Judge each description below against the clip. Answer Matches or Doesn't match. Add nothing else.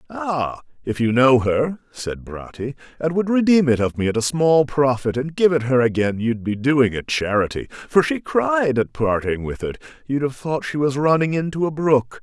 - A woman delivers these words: Doesn't match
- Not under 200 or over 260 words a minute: Matches